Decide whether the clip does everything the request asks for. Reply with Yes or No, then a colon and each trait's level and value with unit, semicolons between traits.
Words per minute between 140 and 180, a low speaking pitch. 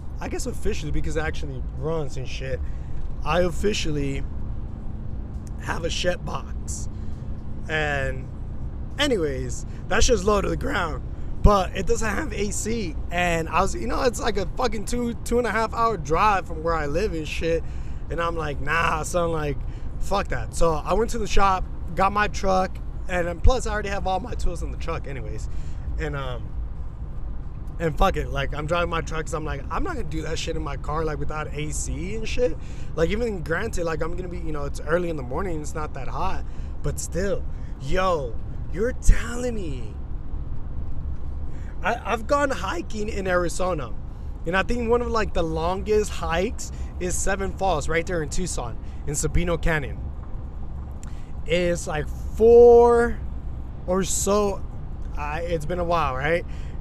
No: average, 175 wpm; medium, 160 Hz